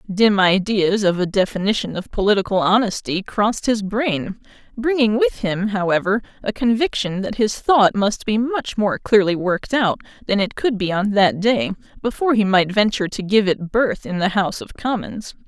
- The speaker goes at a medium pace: Yes, average, 180 wpm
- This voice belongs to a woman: Yes, female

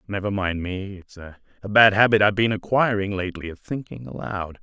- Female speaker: No, male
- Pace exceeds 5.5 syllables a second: Yes, 5.8 syllables/s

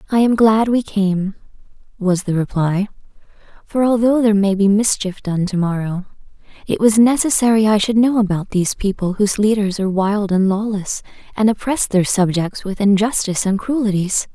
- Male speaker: No, female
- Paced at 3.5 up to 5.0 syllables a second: No, 5.2 syllables/s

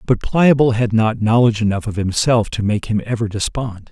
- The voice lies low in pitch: Yes, low, 110 Hz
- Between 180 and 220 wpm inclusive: Yes, average, 200 wpm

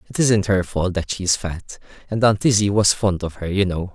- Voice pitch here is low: Yes, very low, 95 Hz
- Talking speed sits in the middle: No, fast, 245 wpm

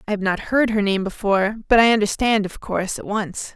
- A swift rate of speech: Yes, fast, 235 wpm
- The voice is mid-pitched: No, high, 205 Hz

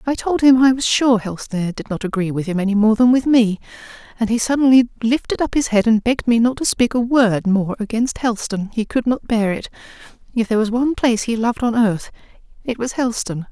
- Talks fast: Yes, fast, 235 wpm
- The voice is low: No, high, 230 Hz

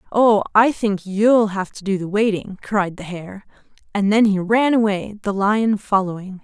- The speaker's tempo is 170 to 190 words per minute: Yes, average, 185 wpm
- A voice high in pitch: Yes, high, 205 Hz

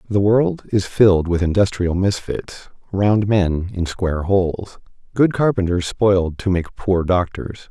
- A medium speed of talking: Yes, average, 150 wpm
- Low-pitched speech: Yes, very low, 95 Hz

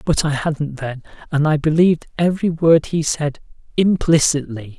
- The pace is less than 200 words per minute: Yes, average, 150 wpm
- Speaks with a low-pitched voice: No, medium, 155 Hz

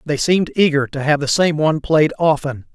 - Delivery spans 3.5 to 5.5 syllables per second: No, 5.7 syllables/s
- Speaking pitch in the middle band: Yes, medium, 150 Hz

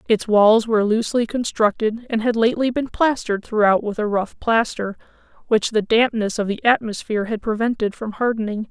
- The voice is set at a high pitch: Yes, high, 220 Hz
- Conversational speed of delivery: Yes, average, 170 wpm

